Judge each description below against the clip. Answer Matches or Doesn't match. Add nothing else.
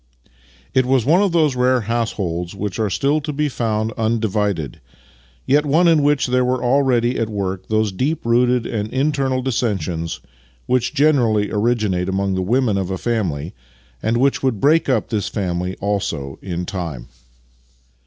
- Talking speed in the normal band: Matches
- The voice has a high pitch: Doesn't match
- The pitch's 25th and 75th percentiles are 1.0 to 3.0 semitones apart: Doesn't match